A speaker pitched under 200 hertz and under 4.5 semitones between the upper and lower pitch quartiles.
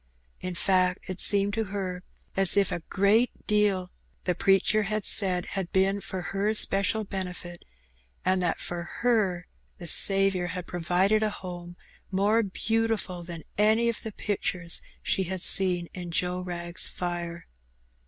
Yes: high, 190 Hz; narrow, 2.4 semitones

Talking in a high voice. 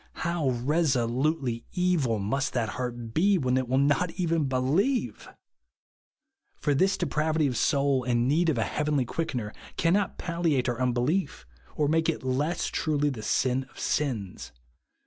No: medium, 140 Hz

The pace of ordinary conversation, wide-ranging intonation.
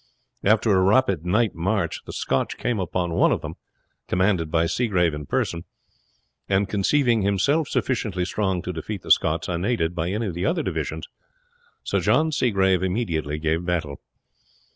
No: average, 160 wpm; average, 4.3 semitones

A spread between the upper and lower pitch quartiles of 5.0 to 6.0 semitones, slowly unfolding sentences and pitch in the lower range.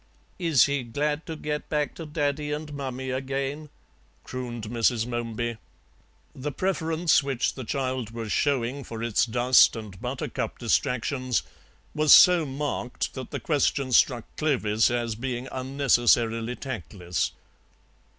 No: average, 3.6 semitones; slow, 130 wpm; low, 130 Hz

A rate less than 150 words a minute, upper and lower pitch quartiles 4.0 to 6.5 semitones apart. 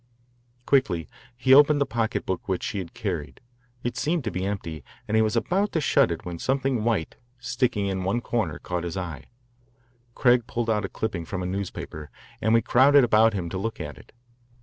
No: average, 195 wpm; average, 5.1 semitones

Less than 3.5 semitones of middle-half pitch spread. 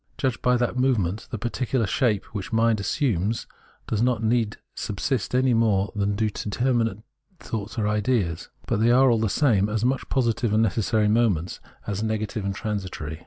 Yes: average, 2.8 semitones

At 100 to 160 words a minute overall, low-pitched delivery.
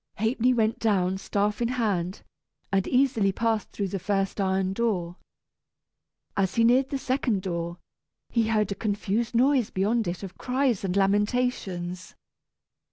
No: average, 145 wpm; high, 205 Hz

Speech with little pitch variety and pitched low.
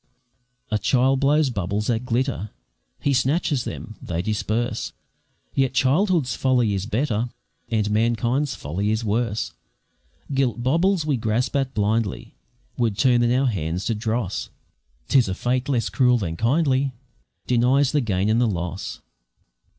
No: average, 3.8 semitones; low, 120 Hz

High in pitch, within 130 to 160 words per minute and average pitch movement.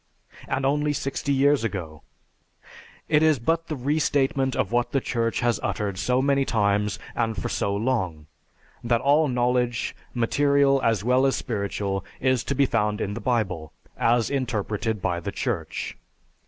No: low, 120 Hz; average, 155 wpm; average, 4.7 semitones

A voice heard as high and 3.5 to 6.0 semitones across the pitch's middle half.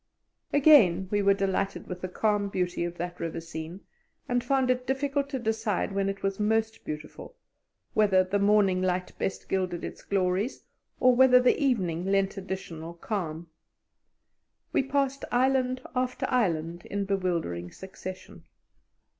Yes: high, 195 Hz; wide, 5.4 semitones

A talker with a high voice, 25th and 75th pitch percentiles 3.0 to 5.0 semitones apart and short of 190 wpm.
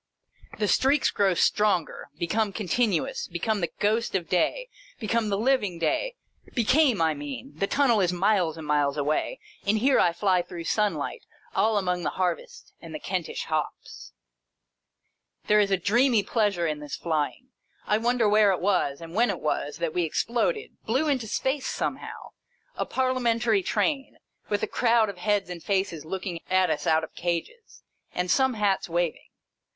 No: high, 200 Hz; wide, 5.4 semitones; average, 175 wpm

